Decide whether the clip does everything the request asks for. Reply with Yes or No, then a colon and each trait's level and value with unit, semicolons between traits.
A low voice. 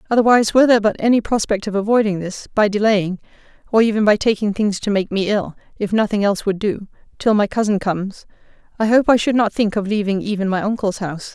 No: high, 210 Hz